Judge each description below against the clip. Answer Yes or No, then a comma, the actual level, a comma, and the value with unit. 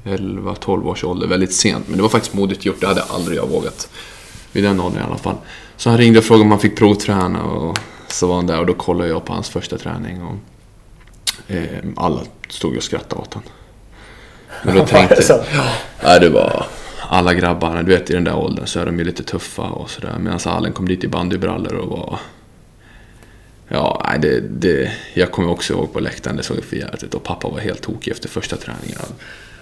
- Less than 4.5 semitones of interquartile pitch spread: Yes, average, 3.0 semitones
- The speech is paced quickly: Yes, fast, 210 wpm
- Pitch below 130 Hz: Yes, low, 100 Hz